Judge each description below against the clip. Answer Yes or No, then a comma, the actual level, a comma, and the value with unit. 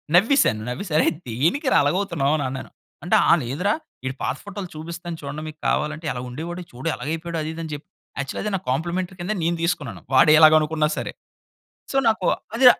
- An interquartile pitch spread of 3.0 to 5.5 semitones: Yes, average, 3.7 semitones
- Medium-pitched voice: Yes, medium, 160 Hz